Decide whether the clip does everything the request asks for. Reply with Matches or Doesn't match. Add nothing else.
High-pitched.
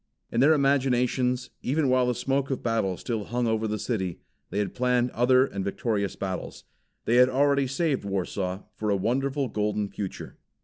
Doesn't match